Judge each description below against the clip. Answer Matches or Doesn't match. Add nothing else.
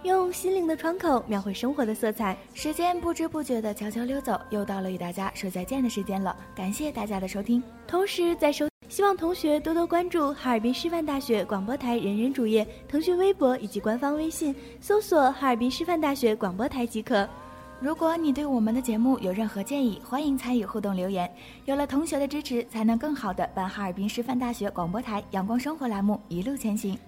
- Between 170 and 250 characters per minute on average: Doesn't match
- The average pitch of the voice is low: Doesn't match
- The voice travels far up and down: Matches